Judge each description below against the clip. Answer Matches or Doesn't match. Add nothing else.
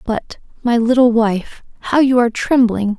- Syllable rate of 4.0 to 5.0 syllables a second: Matches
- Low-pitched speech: Doesn't match